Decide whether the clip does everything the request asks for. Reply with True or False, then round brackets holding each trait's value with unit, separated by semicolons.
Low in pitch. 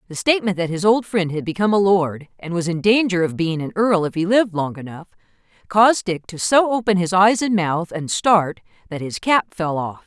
False (185 Hz)